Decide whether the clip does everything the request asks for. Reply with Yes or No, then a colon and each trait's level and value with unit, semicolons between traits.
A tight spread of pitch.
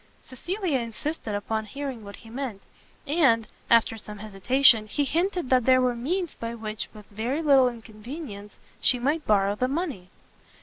No: average, 4.8 semitones